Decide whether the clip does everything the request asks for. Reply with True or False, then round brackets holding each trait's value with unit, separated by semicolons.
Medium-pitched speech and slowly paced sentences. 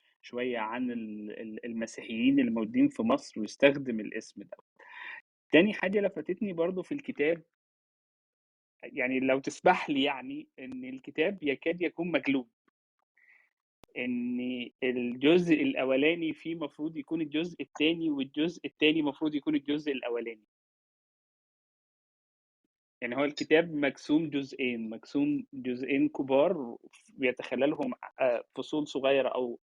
False (155 Hz; 105 wpm)